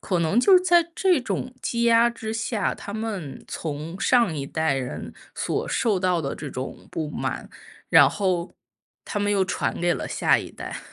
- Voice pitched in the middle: No, high, 200 Hz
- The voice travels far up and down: Yes, wide, 6.4 semitones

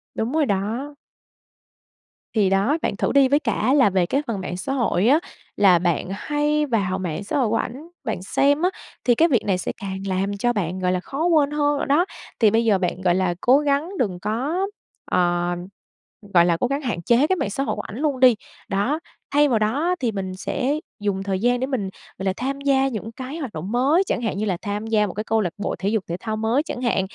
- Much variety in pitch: Yes, wide, 6.3 semitones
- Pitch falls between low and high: No, high, 225 Hz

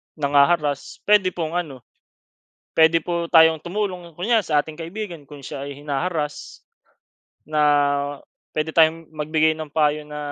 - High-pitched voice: No, medium, 160 Hz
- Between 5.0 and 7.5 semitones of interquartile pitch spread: No, narrow, 2.5 semitones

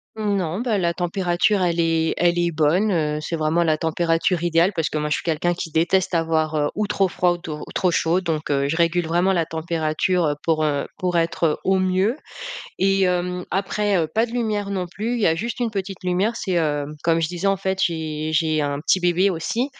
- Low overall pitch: No, medium, 175 Hz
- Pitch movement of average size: Yes, average, 3.0 semitones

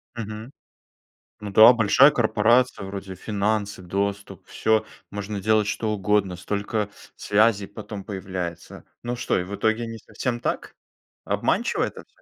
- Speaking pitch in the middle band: No, low, 105 Hz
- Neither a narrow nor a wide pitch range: No, narrow, 1.9 semitones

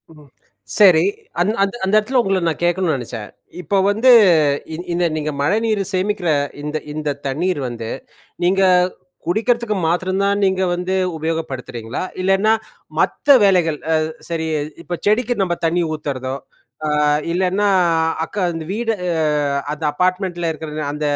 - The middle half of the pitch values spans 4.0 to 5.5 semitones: Yes, average, 4.3 semitones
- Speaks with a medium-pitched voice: Yes, medium, 180 Hz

